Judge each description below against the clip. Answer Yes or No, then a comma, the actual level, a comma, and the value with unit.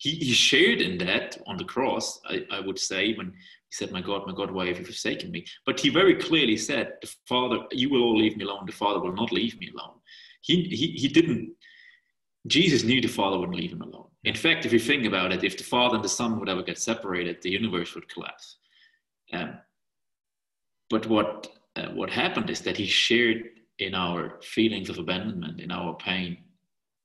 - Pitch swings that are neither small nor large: No, wide, 7.7 semitones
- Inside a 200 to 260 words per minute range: Yes, fast, 205 wpm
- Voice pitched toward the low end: Yes, low, 115 Hz